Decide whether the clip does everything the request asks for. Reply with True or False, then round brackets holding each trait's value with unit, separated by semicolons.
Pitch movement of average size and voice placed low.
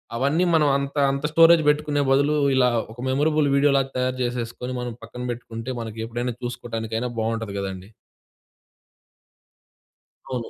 True (3.7 semitones; 125 Hz)